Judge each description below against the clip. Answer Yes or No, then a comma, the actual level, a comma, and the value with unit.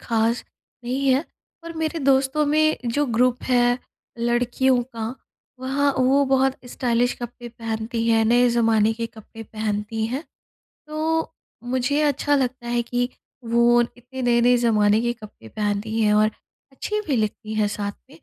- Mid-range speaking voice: No, high, 240 Hz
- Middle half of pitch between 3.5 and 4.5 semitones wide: No, average, 2.8 semitones